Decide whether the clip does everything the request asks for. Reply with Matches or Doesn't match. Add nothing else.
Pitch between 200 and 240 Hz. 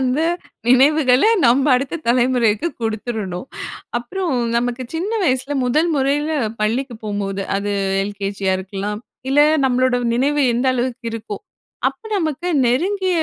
Doesn't match